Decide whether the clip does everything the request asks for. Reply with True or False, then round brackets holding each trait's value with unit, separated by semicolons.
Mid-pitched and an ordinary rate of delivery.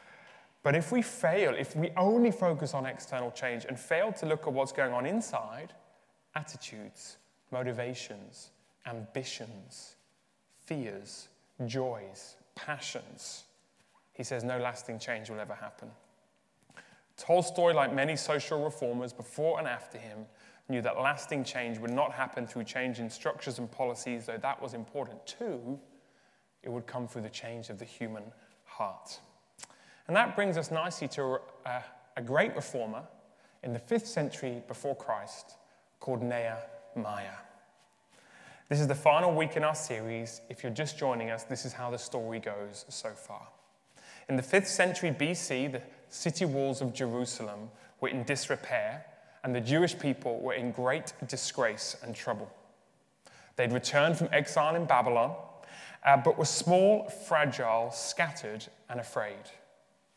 False (130 Hz; 145 wpm)